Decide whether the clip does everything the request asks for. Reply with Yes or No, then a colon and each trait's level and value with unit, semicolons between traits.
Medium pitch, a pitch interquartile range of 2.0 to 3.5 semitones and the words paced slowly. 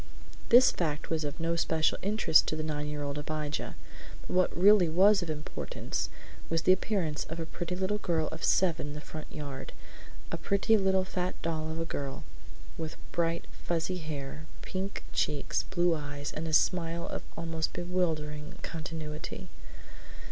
No: medium, 165 Hz; average, 2.9 semitones; average, 165 wpm